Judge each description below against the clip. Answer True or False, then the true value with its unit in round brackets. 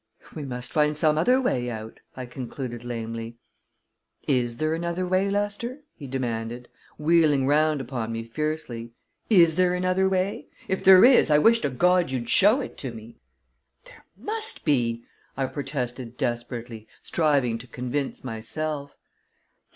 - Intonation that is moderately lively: False (6.6 semitones)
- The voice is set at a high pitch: False (140 Hz)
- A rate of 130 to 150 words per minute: True (145 wpm)